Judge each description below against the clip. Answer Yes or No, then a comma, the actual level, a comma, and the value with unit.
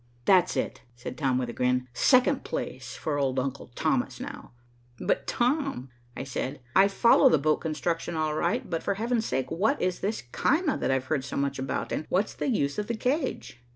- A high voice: No, medium, 160 Hz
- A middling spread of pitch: No, wide, 8.5 semitones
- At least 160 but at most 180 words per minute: No, average, 200 wpm